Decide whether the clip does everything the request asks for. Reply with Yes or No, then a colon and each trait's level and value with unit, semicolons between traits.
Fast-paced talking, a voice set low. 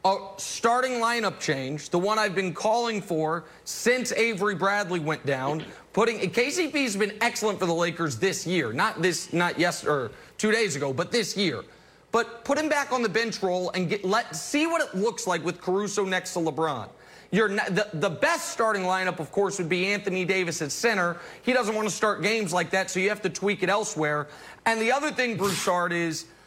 No: fast, 210 wpm; high, 195 Hz